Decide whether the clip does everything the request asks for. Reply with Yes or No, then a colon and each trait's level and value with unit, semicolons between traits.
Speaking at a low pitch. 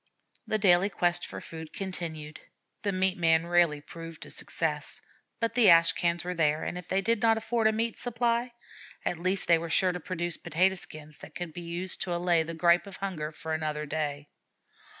No: medium, 175 Hz